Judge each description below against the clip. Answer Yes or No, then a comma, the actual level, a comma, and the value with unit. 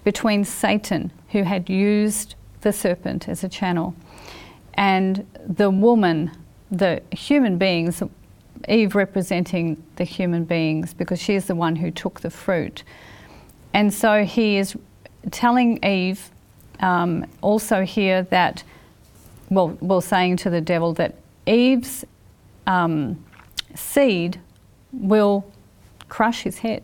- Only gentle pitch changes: No, average, 3.3 semitones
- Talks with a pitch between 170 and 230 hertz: Yes, high, 190 Hz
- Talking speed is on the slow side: Yes, slow, 120 wpm